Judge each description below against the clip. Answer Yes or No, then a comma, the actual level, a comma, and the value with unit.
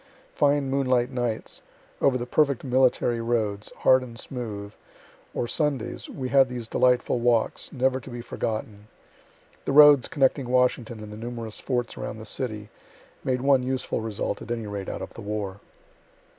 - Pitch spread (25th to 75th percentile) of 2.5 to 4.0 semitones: Yes, average, 2.9 semitones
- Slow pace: No, average, 160 wpm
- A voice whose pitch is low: Yes, low, 120 Hz